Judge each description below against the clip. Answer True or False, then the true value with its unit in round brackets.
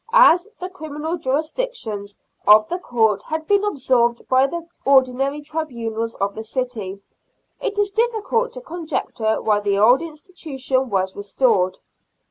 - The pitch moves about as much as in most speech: False (7.6 semitones)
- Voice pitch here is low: False (270 Hz)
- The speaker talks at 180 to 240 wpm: False (140 wpm)